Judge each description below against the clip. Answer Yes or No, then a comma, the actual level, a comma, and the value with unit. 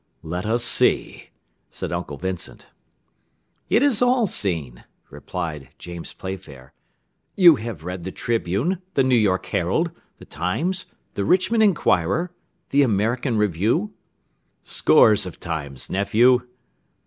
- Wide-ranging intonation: Yes, wide, 8.6 semitones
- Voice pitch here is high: No, low, 105 Hz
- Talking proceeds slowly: Yes, slow, 120 wpm